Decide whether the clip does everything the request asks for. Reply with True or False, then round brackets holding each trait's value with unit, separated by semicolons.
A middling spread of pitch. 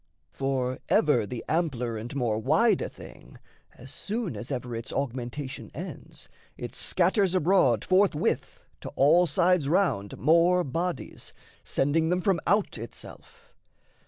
False (6.4 semitones)